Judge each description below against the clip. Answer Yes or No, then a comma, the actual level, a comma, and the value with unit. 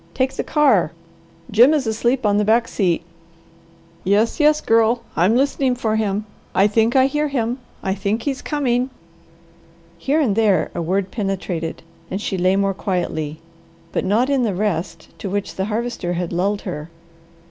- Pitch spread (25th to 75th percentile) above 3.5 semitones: Yes, average, 4.4 semitones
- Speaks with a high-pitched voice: Yes, high, 210 Hz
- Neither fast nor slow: Yes, average, 170 wpm